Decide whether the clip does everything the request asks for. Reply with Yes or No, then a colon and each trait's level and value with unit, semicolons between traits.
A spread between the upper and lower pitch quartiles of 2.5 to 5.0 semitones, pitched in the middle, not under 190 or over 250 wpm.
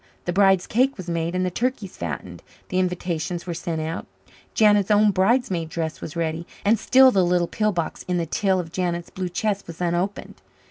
Yes: average, 3.1 semitones; medium, 180 Hz; average, 195 wpm